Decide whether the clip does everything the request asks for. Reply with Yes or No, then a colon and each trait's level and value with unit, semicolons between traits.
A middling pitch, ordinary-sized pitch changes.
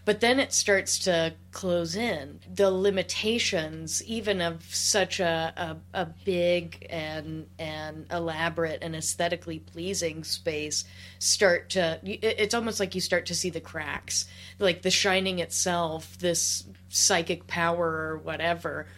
Yes: medium, 170 Hz; average, 3.0 semitones